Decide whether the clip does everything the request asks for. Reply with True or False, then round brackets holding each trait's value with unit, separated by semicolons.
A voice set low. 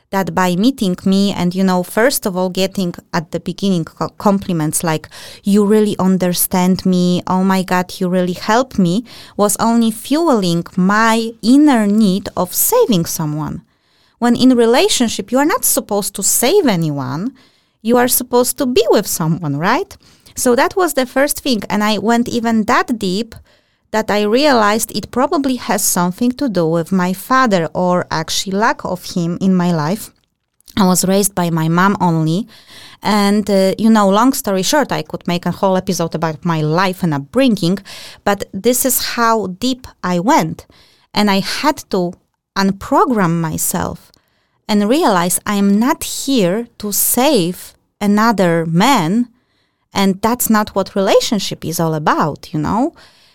False (200 Hz)